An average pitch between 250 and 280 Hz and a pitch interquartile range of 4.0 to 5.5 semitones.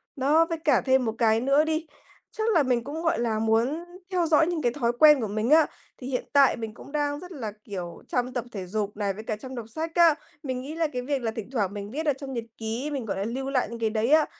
Yes: very high, 255 Hz; average, 5.2 semitones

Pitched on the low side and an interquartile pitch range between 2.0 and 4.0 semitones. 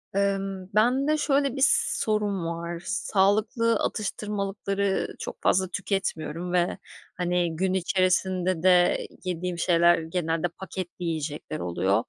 No: medium, 185 Hz; narrow, 2.6 semitones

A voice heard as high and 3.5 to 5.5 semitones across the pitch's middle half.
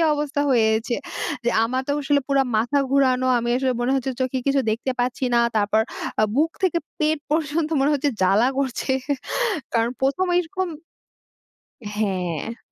Yes: very high, 265 Hz; average, 3.8 semitones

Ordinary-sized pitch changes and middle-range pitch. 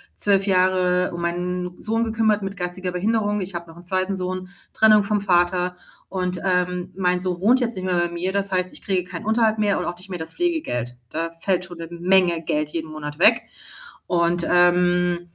No: narrow, 2.1 semitones; medium, 180 Hz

